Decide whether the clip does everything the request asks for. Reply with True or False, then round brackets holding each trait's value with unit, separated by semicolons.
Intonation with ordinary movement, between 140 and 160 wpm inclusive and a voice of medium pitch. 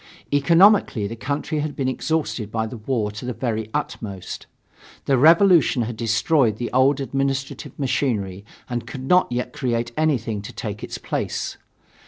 False (4.3 semitones; 155 wpm; 125 Hz)